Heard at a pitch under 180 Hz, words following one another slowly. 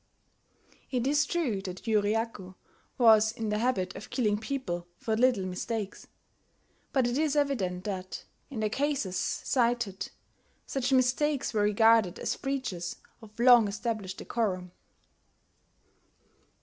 No: high, 225 Hz; slow, 125 wpm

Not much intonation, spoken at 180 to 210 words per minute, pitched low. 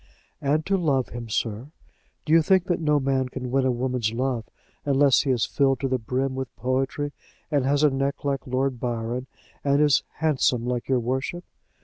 Yes: narrow, 2.3 semitones; average, 195 wpm; low, 130 Hz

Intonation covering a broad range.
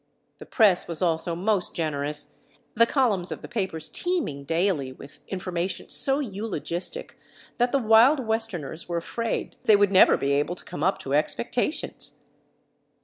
Yes: wide, 5.8 semitones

